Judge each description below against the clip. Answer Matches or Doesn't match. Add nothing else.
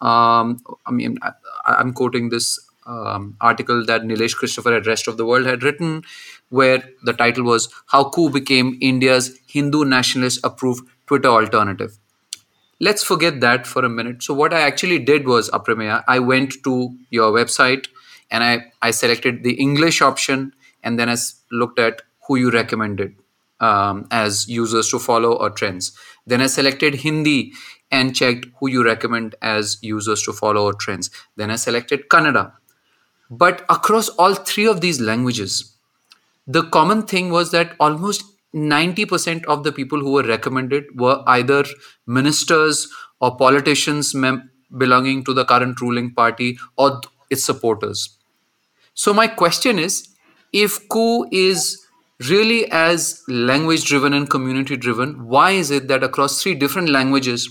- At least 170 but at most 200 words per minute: Doesn't match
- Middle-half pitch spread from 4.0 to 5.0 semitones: Matches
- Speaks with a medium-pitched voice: Doesn't match